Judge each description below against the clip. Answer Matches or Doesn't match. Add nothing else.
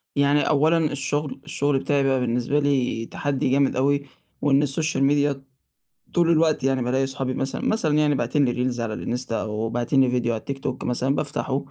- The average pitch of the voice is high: Doesn't match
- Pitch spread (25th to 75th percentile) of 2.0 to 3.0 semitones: Matches